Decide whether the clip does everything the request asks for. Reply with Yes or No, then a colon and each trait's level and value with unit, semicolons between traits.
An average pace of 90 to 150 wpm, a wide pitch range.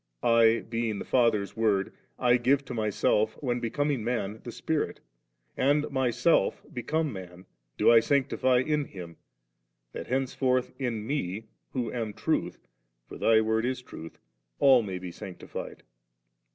No: average, 145 wpm; average, 3.6 semitones